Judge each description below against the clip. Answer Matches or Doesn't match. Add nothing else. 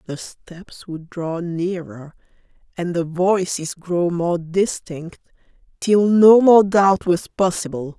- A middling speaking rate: Doesn't match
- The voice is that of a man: Doesn't match